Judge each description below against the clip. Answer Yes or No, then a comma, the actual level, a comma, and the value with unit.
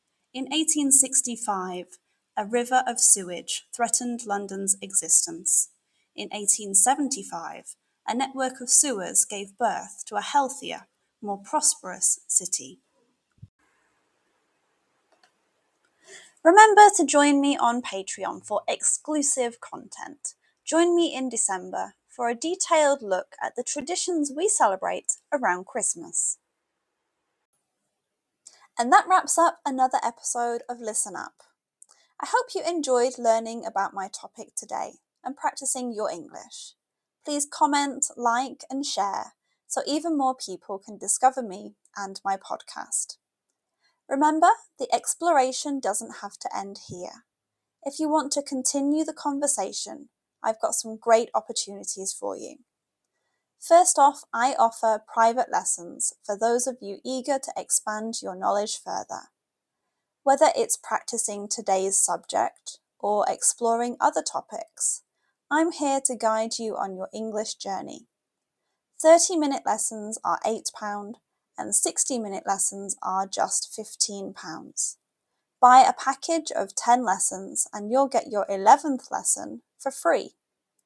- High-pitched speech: Yes, very high, 250 Hz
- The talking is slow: Yes, slow, 125 wpm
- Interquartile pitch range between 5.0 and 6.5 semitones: Yes, wide, 5.5 semitones